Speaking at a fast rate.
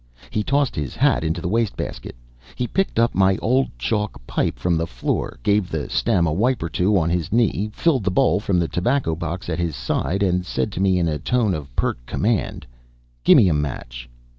Yes: fast, 215 wpm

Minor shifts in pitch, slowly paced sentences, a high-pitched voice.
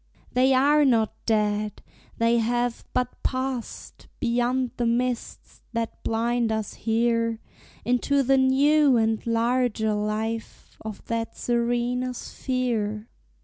Yes: narrow, 2.1 semitones; slow, 110 wpm; high, 235 Hz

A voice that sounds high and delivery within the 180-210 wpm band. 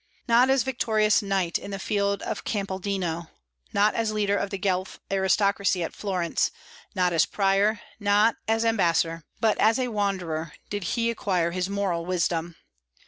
No: high, 200 Hz; average, 155 wpm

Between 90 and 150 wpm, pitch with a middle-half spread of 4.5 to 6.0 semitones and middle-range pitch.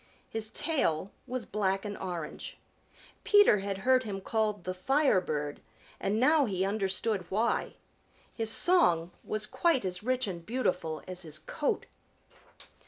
No: slow, 135 wpm; average, 5.3 semitones; high, 205 Hz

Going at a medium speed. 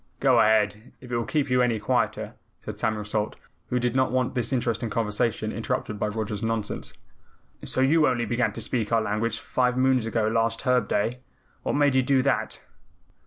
Yes: average, 190 wpm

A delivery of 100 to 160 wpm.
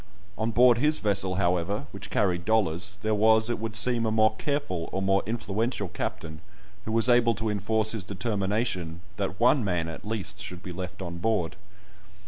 No: average, 180 wpm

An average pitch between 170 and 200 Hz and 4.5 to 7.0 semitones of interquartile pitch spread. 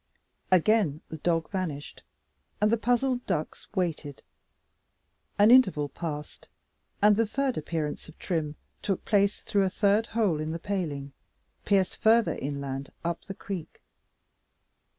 Yes: medium, 185 Hz; wide, 5.4 semitones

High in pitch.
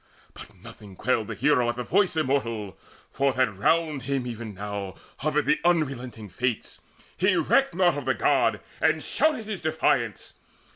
No: low, 130 Hz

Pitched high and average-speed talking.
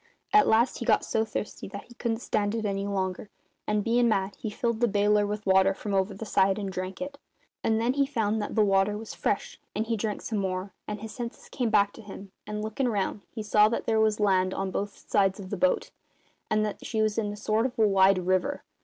No: high, 210 Hz; fast, 240 wpm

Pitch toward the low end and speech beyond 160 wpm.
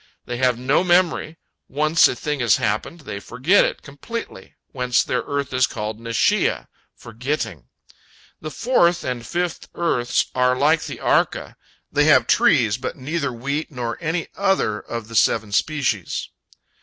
No: low, 130 Hz; average, 150 wpm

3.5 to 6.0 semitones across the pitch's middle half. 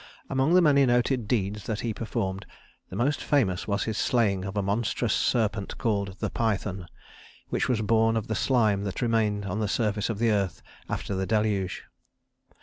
No: average, 2.8 semitones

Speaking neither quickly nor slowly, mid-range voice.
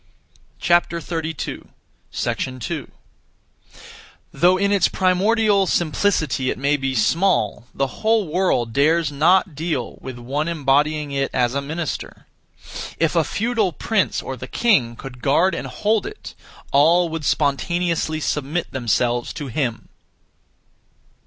No: slow, 120 wpm; medium, 155 Hz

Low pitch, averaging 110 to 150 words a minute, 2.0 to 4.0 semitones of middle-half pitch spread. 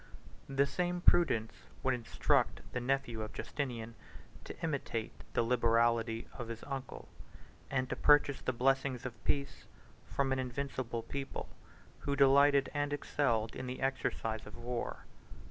Yes: low, 130 Hz; average, 140 wpm; average, 3.1 semitones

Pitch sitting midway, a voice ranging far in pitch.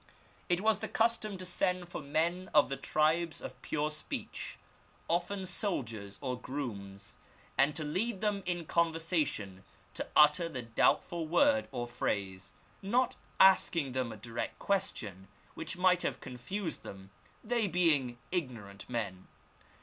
Yes: medium, 155 Hz; wide, 7.3 semitones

